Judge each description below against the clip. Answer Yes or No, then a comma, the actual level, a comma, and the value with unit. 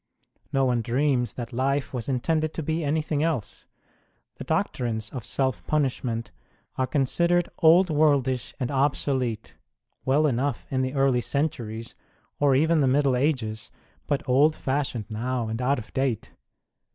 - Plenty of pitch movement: No, average, 3.2 semitones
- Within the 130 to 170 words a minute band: Yes, average, 155 wpm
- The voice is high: No, low, 135 Hz